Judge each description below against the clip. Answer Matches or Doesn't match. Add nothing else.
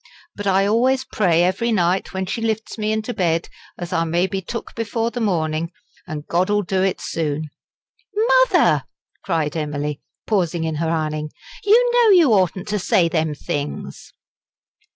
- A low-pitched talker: Doesn't match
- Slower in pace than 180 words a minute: Matches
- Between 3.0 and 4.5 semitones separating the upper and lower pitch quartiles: Doesn't match